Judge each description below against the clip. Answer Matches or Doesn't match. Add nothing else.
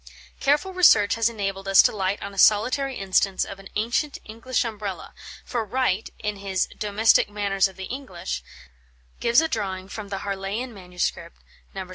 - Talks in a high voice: Matches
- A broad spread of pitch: Doesn't match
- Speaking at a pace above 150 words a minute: Matches